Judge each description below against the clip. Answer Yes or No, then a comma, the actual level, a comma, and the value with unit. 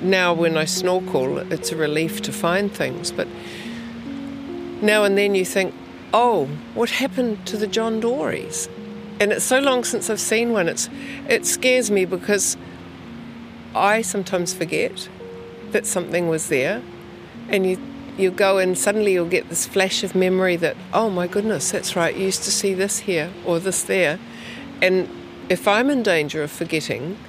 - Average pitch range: Yes, average, 3.5 semitones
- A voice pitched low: No, high, 195 Hz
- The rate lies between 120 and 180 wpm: Yes, average, 170 wpm